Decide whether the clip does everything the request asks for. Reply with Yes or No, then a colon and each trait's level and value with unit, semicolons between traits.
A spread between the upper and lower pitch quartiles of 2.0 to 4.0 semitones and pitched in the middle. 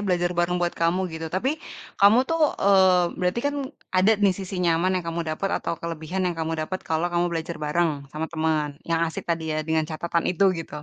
Yes: narrow, 2.4 semitones; medium, 170 Hz